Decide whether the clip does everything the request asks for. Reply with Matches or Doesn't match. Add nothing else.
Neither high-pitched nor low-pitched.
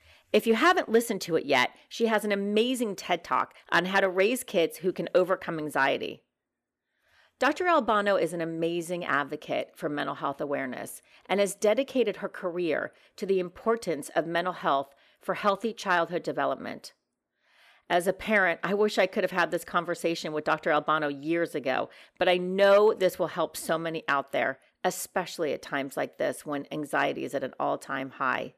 Matches